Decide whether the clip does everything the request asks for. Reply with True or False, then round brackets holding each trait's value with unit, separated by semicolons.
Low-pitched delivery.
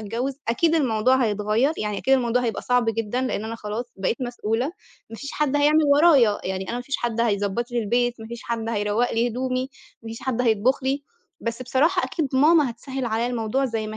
False (240 Hz)